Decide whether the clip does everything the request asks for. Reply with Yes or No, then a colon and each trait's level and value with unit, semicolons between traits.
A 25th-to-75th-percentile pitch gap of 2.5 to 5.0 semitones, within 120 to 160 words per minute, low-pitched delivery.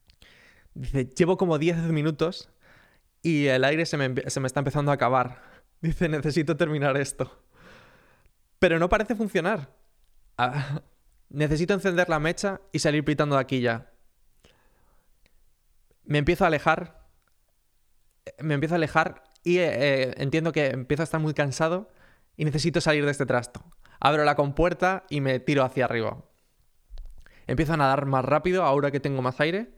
No: average, 3.8 semitones; average, 155 wpm; medium, 150 Hz